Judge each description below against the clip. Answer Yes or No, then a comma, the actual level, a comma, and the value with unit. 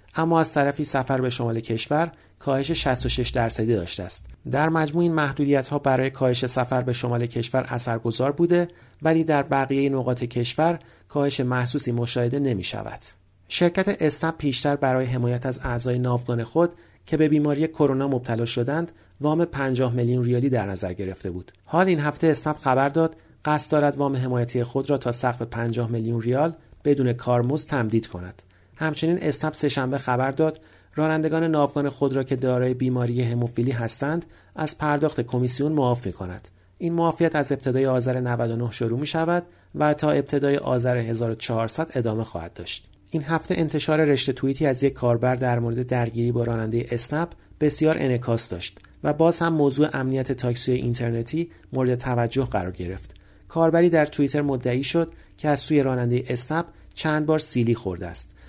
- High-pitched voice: No, low, 130 Hz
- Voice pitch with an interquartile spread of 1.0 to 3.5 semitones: No, average, 4.1 semitones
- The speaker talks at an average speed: No, fast, 160 wpm